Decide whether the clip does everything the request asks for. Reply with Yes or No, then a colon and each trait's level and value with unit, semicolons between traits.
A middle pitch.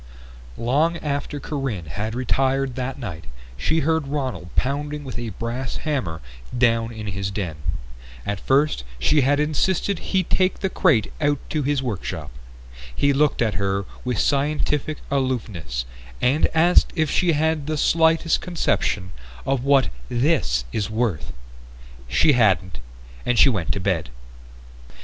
No: low, 130 Hz